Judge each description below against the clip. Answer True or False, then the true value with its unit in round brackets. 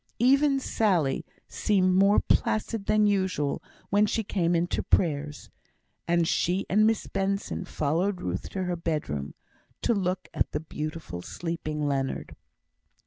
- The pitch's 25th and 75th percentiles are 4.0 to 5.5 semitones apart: True (4.7 semitones)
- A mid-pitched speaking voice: True (180 Hz)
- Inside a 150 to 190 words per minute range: False (140 wpm)